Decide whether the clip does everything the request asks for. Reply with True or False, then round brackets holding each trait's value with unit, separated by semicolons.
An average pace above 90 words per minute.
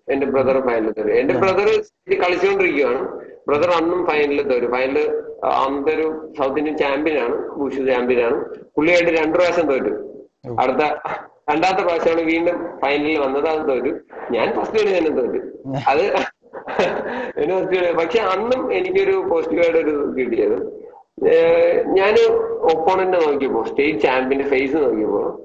True (120 wpm)